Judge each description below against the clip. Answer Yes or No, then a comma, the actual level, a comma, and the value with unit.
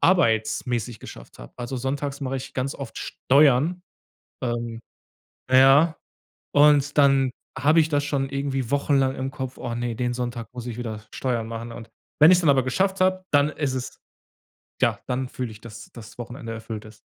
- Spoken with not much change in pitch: No, average, 3.3 semitones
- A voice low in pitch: Yes, low, 130 Hz